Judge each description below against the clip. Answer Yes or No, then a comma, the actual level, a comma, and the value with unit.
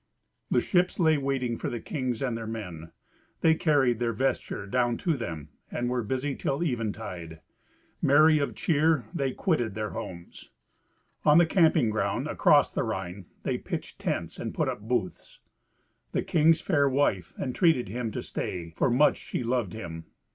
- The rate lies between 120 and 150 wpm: No, average, 165 wpm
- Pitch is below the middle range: Yes, low, 125 Hz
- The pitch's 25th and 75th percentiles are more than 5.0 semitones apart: Yes, wide, 5.6 semitones